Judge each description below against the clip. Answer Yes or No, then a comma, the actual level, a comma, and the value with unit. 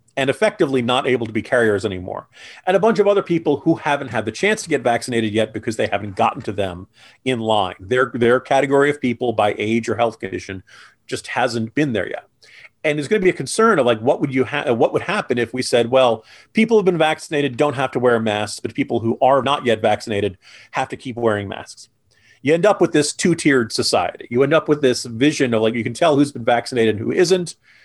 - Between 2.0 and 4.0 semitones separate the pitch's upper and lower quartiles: No, average, 4.8 semitones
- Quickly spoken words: Yes, fast, 235 wpm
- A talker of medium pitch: No, low, 125 Hz